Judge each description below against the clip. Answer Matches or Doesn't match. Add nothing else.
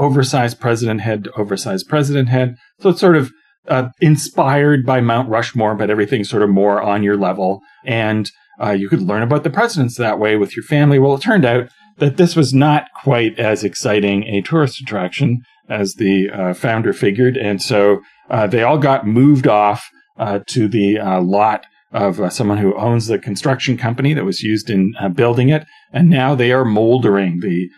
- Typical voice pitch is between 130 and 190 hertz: Doesn't match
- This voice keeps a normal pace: Matches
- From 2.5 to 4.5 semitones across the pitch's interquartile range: Doesn't match